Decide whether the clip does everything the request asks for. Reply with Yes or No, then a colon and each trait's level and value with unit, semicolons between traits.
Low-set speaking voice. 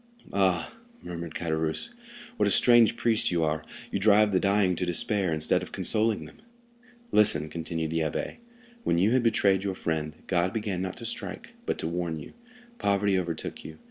Yes: very low, 90 Hz